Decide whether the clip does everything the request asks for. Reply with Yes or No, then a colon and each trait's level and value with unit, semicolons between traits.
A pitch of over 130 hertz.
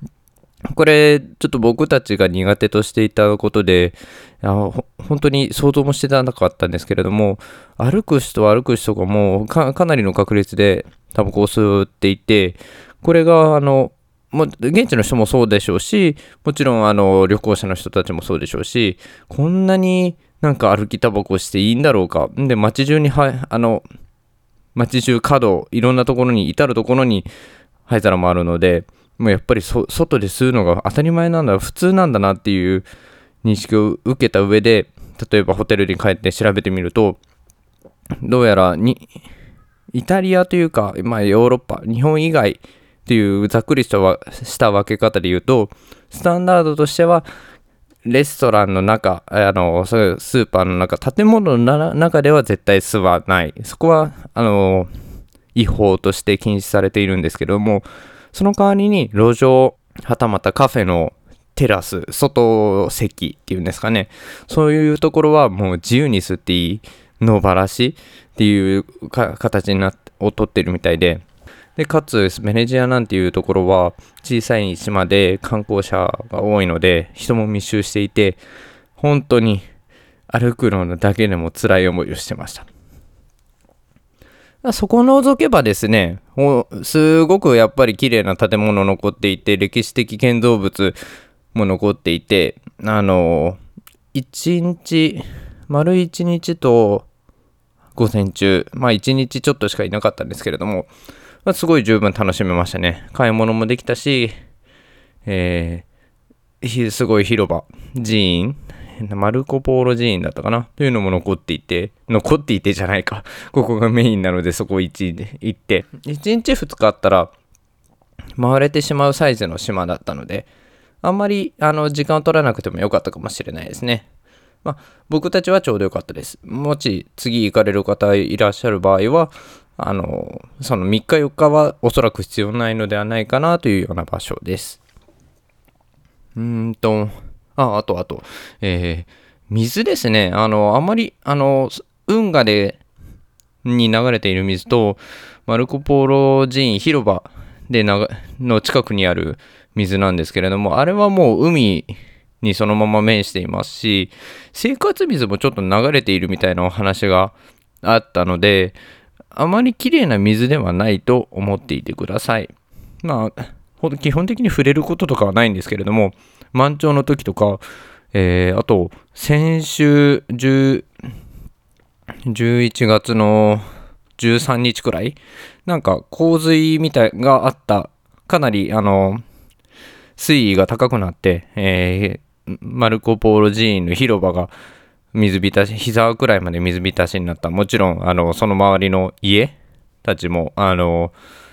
No: low, 110 Hz